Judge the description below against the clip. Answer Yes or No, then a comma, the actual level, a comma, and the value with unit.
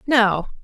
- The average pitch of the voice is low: No, high, 215 Hz